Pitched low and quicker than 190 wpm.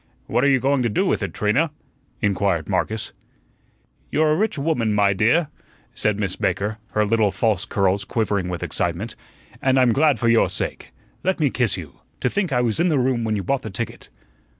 Yes: low, 115 Hz; average, 200 wpm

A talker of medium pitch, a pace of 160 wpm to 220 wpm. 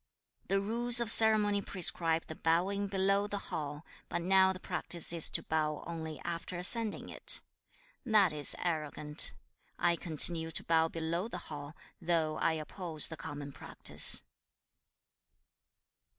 No: medium, 170 Hz; average, 140 wpm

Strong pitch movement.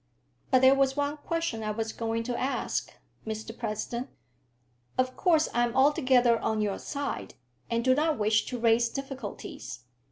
No: average, 3.5 semitones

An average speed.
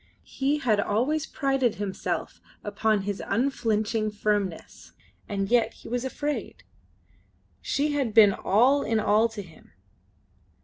No: slow, 125 wpm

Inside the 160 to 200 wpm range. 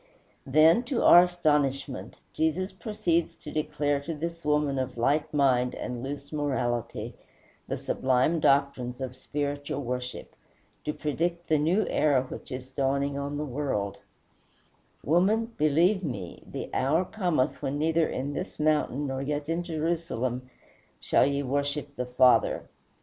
No: average, 140 wpm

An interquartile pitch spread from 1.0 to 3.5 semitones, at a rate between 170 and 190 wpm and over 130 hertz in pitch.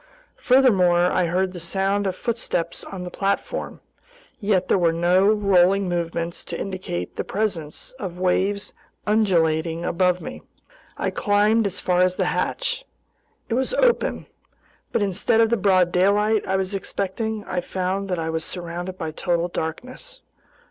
No: average, 2.8 semitones; average, 155 wpm; medium, 185 Hz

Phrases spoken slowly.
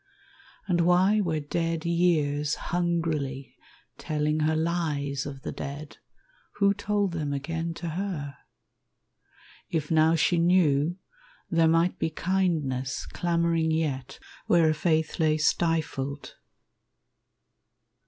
Yes: slow, 110 wpm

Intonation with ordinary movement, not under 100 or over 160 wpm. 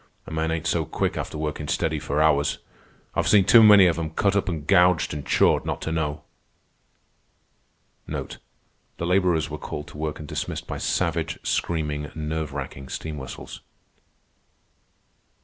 No: narrow, 2.2 semitones; average, 155 wpm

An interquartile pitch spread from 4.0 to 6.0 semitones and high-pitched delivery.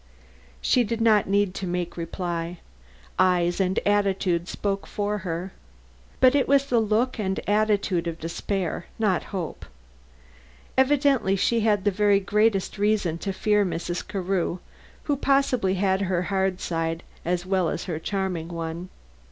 No: average, 3.1 semitones; high, 195 Hz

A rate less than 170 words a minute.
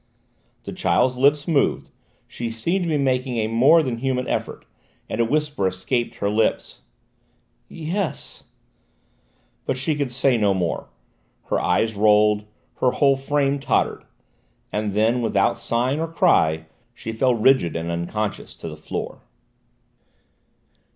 Yes: average, 140 wpm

